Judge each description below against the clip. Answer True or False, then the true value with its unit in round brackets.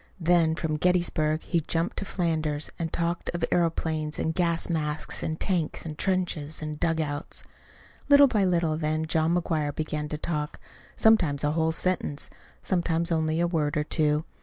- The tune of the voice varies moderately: False (2.1 semitones)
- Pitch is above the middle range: False (160 Hz)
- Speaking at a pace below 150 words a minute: False (160 wpm)